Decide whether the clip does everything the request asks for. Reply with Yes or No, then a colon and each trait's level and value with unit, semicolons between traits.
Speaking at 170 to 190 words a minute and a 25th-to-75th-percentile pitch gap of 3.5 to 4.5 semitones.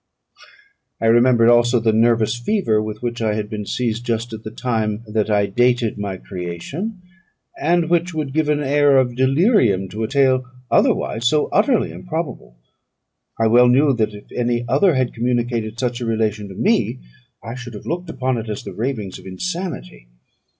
Yes: average, 180 wpm; average, 3.8 semitones